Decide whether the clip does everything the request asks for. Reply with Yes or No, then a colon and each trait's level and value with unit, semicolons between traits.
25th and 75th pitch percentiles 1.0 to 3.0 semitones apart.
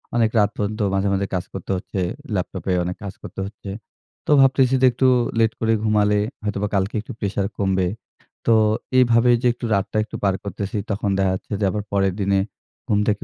Yes: narrow, 2.4 semitones